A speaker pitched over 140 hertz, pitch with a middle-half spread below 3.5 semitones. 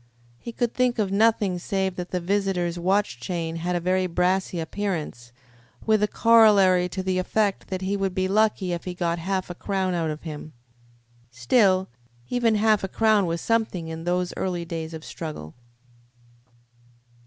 Yes: medium, 185 Hz; average, 3.0 semitones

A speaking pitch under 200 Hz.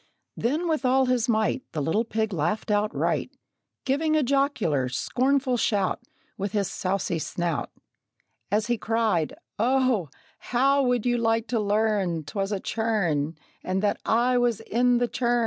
No: high, 225 Hz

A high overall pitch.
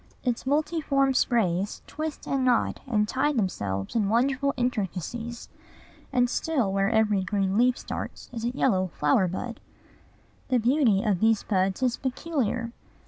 Yes: high, 235 Hz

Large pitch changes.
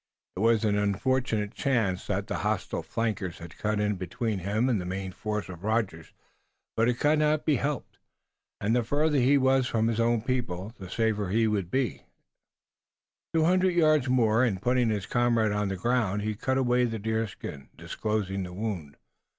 No: average, 3.9 semitones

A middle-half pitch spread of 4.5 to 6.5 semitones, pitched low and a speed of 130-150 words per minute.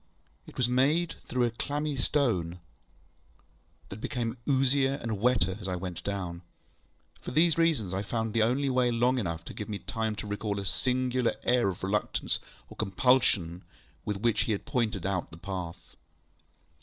No: average, 4.8 semitones; low, 115 Hz; average, 165 wpm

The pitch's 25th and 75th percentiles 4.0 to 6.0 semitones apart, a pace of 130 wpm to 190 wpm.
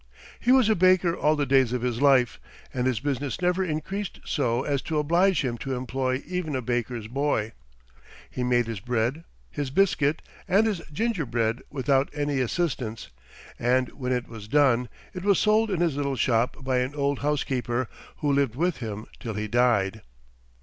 Yes: average, 4.3 semitones; average, 175 wpm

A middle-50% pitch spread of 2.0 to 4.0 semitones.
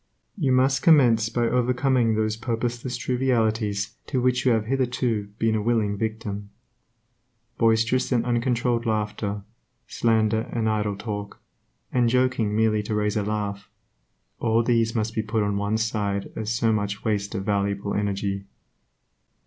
Yes: narrow, 2.5 semitones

